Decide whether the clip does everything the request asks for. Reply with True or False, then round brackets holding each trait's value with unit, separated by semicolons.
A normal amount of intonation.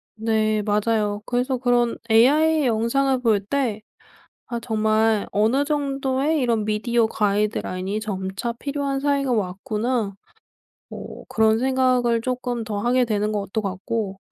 True (3.3 semitones)